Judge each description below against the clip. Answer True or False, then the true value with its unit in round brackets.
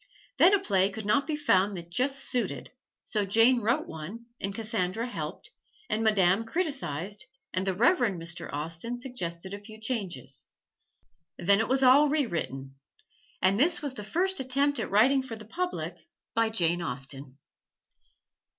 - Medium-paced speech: True (155 wpm)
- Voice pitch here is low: False (215 Hz)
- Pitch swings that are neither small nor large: False (6.5 semitones)